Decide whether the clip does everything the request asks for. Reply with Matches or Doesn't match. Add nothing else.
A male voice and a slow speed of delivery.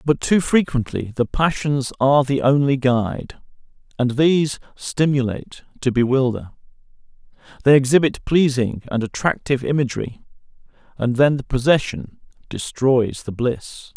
Matches